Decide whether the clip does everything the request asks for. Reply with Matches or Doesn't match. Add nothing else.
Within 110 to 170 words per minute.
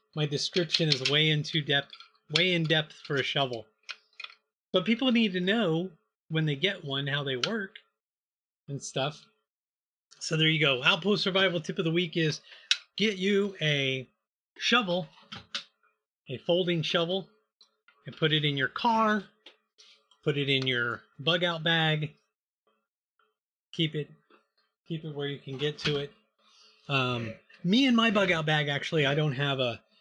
Matches